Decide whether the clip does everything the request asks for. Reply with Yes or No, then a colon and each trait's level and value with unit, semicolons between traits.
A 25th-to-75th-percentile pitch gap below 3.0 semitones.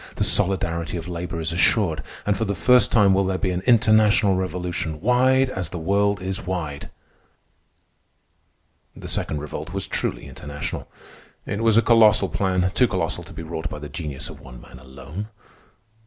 No: average, 4.3 semitones